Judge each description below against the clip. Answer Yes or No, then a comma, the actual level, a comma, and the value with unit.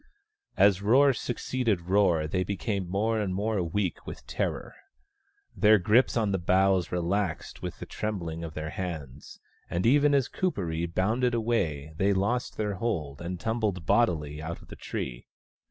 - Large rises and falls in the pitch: No, average, 4.6 semitones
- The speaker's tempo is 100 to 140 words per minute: No, average, 155 wpm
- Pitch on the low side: Yes, very low, 95 Hz